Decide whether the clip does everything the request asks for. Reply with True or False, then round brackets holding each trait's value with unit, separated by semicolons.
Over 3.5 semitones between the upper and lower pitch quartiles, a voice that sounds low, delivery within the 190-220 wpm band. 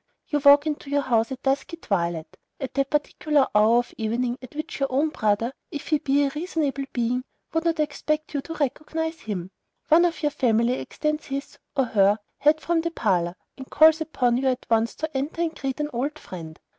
False (4.4 semitones; 275 Hz; 205 wpm)